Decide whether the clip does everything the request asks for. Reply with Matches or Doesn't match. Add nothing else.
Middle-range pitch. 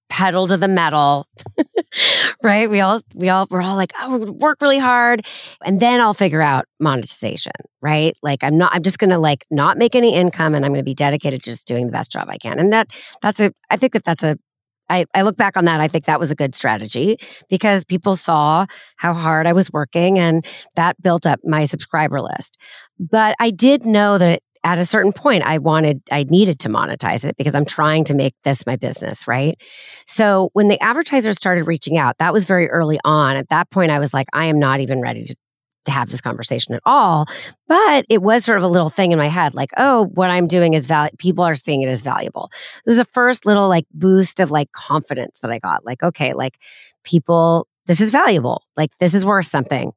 Matches